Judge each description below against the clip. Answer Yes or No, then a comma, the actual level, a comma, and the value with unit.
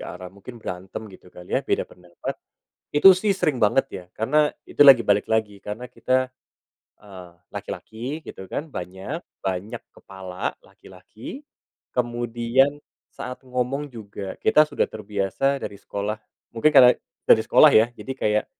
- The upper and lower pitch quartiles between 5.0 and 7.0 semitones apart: Yes, average, 5.3 semitones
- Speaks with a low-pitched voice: Yes, low, 110 Hz